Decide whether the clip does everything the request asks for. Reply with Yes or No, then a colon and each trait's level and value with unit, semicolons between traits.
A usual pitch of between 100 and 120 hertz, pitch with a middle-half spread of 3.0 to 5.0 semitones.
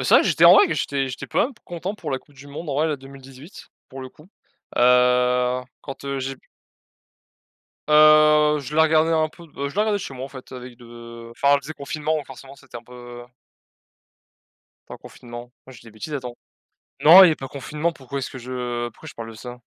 No: low, 135 Hz; average, 3.4 semitones